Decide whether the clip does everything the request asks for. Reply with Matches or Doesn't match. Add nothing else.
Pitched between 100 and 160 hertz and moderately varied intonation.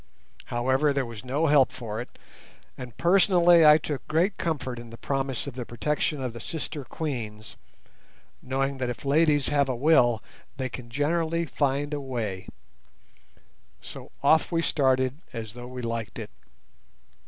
Matches